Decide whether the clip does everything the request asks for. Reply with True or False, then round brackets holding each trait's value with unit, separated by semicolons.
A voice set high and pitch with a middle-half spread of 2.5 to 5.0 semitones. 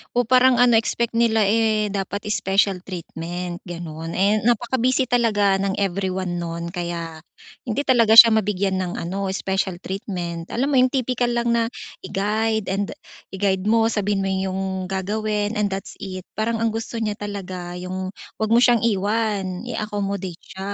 True (200 Hz; 3.1 semitones)